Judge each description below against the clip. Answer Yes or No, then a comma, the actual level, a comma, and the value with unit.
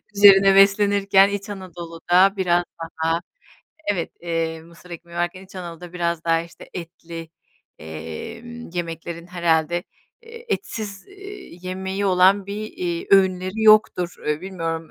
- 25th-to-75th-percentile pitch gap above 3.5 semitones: No, average, 2.8 semitones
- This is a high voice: No, medium, 180 Hz